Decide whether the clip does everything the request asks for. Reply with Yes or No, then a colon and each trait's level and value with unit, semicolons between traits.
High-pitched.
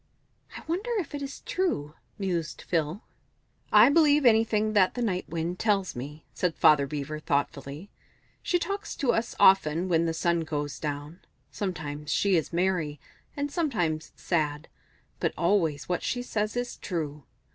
No: medium, 180 Hz